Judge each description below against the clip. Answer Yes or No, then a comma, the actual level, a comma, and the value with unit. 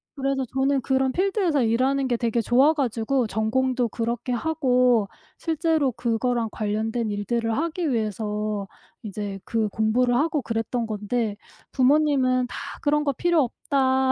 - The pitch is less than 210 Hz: No, very high, 250 Hz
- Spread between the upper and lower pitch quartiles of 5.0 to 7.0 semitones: No, average, 3.5 semitones